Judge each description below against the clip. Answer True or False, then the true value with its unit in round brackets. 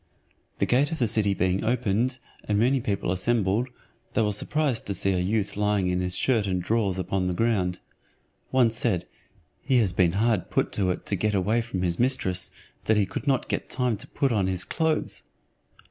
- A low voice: True (105 Hz)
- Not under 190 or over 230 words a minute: True (200 wpm)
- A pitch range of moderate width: True (4.3 semitones)